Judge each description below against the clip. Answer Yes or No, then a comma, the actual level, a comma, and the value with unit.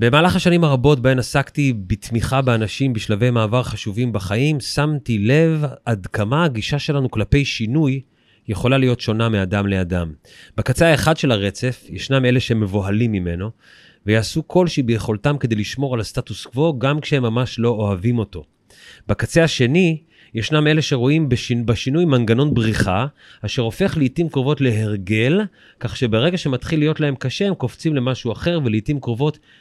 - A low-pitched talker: Yes, low, 125 Hz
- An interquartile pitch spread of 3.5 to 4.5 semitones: No, average, 4.9 semitones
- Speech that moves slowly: No, average, 145 wpm